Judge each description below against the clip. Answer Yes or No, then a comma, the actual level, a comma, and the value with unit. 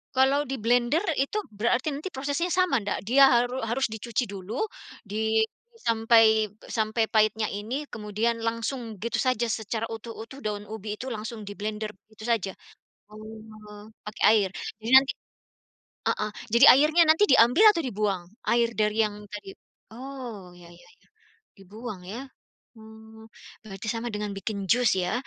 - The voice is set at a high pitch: Yes, high, 220 Hz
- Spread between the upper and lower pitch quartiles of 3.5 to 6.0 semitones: No, average, 2.7 semitones